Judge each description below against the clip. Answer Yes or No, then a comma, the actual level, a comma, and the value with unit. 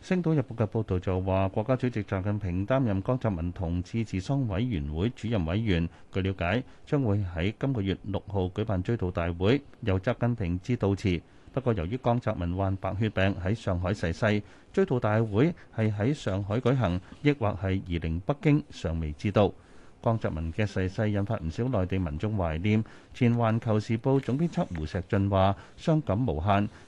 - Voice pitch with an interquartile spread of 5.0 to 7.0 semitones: No, average, 4.4 semitones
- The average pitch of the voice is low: Yes, low, 105 Hz